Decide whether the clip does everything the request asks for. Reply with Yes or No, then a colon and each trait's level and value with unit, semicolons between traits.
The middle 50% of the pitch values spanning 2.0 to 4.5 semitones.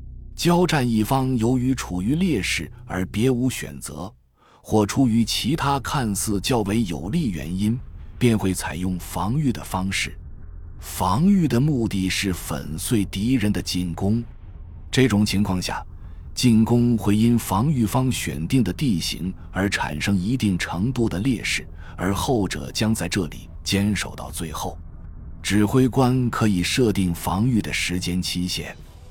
No: wide, 5.6 semitones